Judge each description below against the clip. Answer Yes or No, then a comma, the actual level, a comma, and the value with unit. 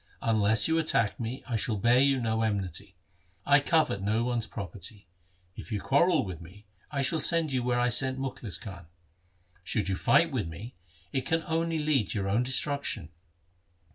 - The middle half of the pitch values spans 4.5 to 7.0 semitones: Yes, wide, 5.5 semitones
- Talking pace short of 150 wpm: No, average, 180 wpm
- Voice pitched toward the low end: Yes, low, 120 Hz